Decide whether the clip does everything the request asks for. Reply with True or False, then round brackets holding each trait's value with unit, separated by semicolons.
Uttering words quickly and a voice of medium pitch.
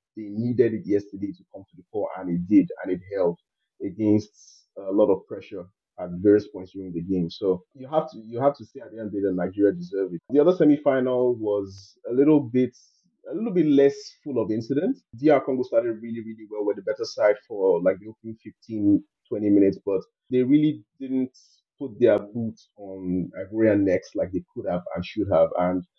False (215 wpm; 110 Hz)